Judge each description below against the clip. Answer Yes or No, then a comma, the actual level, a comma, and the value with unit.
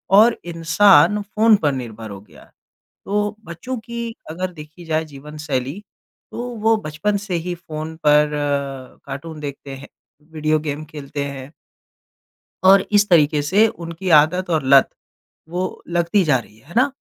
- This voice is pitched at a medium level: Yes, medium, 160 Hz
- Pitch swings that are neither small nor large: Yes, average, 4.9 semitones